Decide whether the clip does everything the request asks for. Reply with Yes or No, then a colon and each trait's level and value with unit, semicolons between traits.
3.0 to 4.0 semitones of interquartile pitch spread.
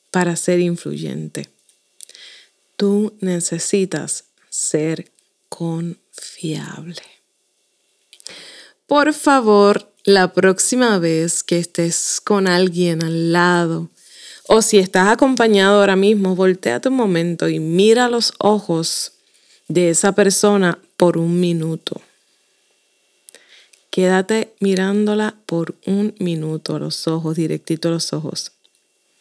Yes: average, 3.5 semitones